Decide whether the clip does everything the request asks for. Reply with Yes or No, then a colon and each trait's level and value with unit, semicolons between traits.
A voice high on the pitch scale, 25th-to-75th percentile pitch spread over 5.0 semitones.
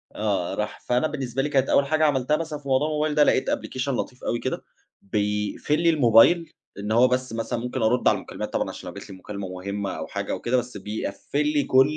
No: low, 125 Hz; wide, 5.5 semitones